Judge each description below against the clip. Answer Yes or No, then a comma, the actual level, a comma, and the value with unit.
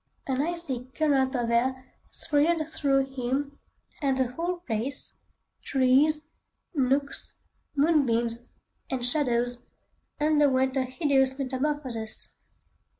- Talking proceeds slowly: Yes, slow, 90 wpm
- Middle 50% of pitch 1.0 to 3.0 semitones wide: Yes, average, 2.7 semitones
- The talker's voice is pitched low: No, very high, 270 Hz